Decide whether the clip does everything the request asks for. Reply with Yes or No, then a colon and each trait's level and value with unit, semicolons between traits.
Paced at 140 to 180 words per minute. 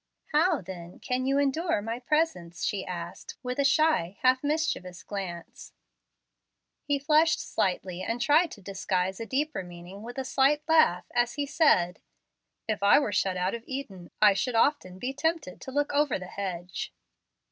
Yes: average, 170 wpm